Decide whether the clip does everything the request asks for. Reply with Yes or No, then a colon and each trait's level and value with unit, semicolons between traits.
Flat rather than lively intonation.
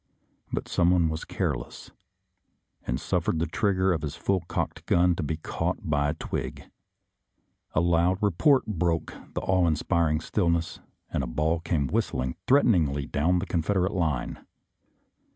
No: average, 3.0 semitones